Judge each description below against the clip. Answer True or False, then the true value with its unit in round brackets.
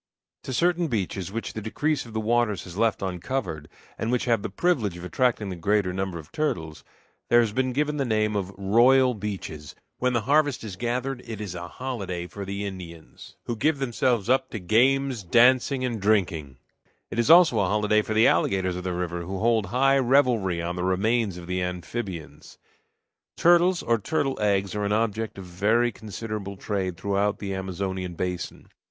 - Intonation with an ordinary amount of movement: True (4.7 semitones)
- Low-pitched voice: True (105 Hz)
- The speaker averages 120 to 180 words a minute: False (190 wpm)